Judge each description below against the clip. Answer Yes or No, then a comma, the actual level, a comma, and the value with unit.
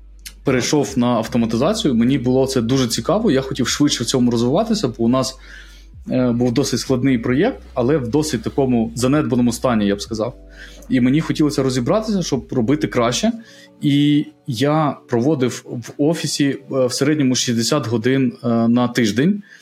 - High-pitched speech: No, low, 130 Hz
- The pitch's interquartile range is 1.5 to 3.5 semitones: Yes, average, 3.2 semitones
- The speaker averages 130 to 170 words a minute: Yes, average, 145 wpm